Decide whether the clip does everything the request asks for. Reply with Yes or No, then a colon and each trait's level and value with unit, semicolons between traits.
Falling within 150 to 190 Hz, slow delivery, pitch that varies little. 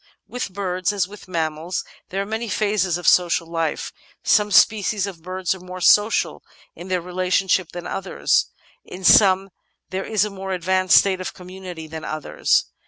No: medium, 185 Hz; average, 170 wpm; narrow, 1.9 semitones